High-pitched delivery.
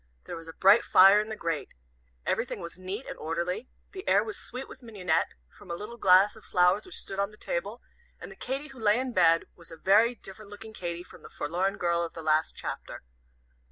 Yes: high, 195 Hz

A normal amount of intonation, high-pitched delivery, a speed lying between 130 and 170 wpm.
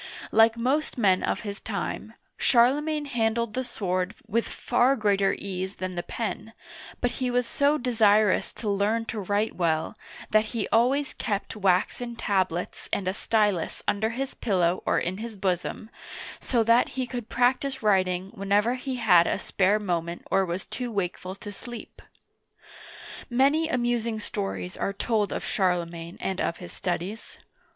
Yes: average, 4.3 semitones; high, 215 Hz; average, 155 wpm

